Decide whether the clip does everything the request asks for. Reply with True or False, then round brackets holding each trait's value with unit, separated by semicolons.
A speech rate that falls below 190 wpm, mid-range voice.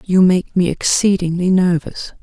True (135 wpm; 180 Hz)